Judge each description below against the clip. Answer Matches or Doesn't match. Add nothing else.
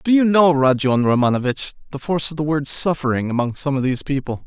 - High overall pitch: Doesn't match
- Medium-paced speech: Doesn't match